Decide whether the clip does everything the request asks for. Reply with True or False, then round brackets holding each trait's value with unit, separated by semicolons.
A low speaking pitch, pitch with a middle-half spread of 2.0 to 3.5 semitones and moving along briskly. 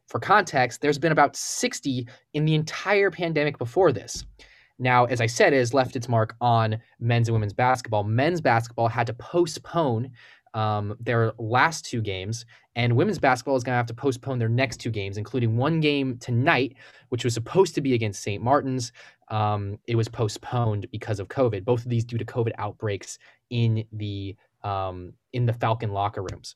False (120 Hz; 3.0 semitones; 190 wpm)